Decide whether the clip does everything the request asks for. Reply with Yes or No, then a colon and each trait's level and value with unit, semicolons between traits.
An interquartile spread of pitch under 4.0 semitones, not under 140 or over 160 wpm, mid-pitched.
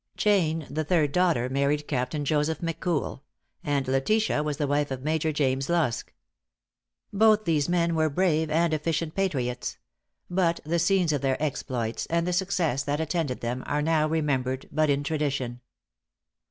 Yes: average, 3.3 semitones; average, 155 wpm; medium, 155 Hz